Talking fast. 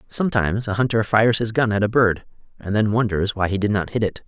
Yes: fast, 255 wpm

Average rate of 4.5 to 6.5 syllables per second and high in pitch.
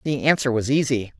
No: 5.6 syllables/s; low, 130 Hz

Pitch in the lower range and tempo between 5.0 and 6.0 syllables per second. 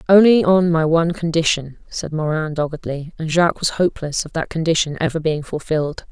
No: medium, 160 Hz; 5.7 syllables/s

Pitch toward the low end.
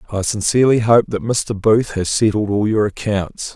Yes: low, 105 Hz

